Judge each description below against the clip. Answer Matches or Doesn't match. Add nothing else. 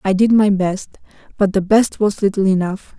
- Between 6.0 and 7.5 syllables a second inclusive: Doesn't match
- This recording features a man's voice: Doesn't match